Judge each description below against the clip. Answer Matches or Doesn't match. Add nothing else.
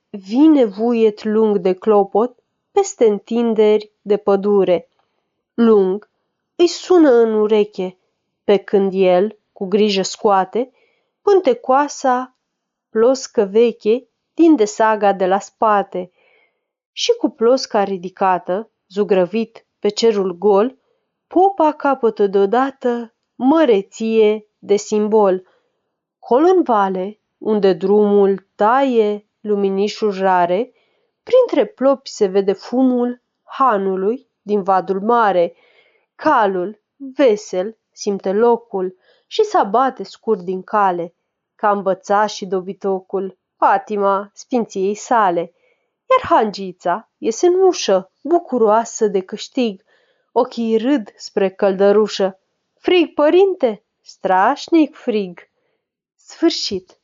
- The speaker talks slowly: Matches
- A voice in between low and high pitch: Doesn't match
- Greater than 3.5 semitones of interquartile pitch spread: Matches